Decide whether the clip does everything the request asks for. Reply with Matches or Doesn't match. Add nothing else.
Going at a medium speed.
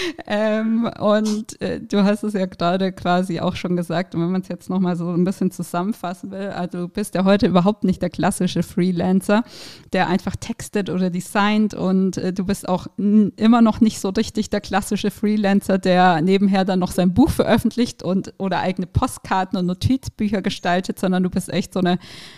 Doesn't match